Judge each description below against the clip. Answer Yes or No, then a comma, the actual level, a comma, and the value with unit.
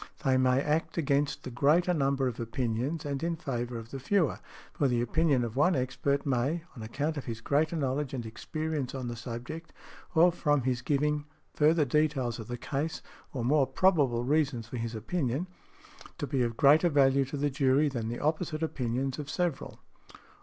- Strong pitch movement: No, average, 3.8 semitones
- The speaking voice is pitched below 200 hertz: Yes, medium, 140 Hz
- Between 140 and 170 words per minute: No, average, 180 wpm